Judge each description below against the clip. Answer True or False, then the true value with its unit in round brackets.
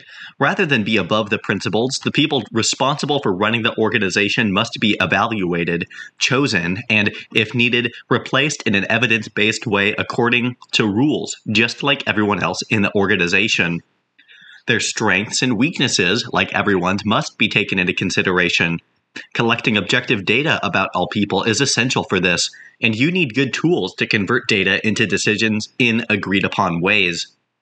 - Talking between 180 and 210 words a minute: False (155 wpm)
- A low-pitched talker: True (110 Hz)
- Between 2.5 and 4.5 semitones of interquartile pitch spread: True (3.3 semitones)